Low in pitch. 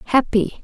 No: high, 230 Hz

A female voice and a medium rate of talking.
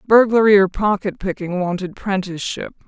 No: female; slow, 125 wpm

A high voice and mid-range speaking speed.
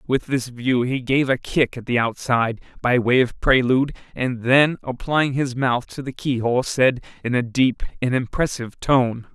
No: low, 125 Hz; average, 185 wpm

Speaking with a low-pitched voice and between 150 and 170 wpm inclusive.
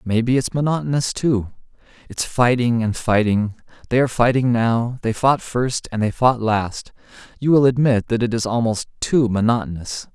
Yes: low, 120 Hz; average, 165 wpm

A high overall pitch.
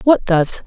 Yes: high, 205 Hz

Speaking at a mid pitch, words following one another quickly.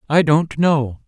No: medium, 150 Hz; average, 170 wpm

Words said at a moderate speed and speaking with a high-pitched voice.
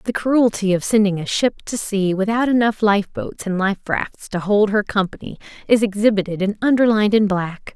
Yes: average, 195 wpm; high, 205 Hz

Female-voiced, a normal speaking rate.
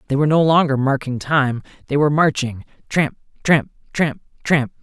No: male; average, 160 wpm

